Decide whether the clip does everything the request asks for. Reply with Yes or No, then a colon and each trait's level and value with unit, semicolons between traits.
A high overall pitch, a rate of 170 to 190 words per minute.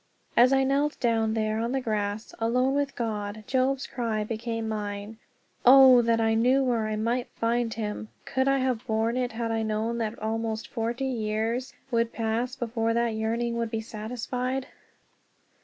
Yes: high, 230 Hz; average, 175 wpm